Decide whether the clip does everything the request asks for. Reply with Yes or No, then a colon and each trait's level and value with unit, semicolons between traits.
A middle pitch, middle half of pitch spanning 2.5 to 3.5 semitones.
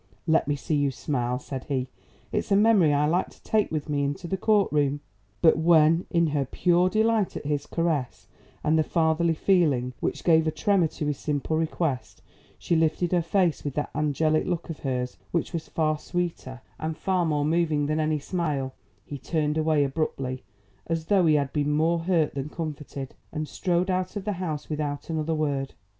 Yes: medium, 155 Hz; average, 2.8 semitones